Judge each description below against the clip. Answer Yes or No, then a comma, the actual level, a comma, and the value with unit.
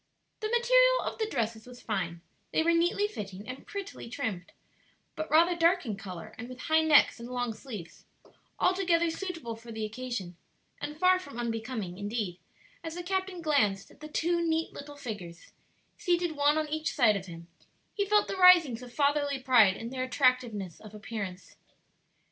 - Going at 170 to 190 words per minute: Yes, average, 175 wpm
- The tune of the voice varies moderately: No, wide, 7.5 semitones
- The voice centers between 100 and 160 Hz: No, very high, 260 Hz